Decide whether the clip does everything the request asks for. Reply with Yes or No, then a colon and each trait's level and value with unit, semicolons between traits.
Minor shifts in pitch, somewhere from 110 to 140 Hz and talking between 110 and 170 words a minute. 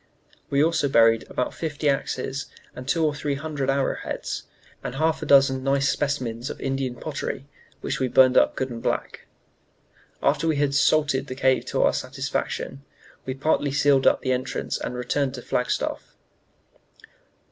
Yes: narrow, 1.9 semitones; low, 135 Hz; average, 165 wpm